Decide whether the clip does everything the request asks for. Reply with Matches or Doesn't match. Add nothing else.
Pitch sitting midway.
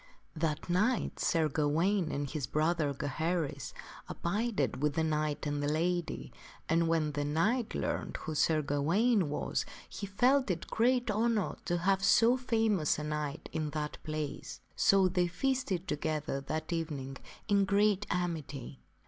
Matches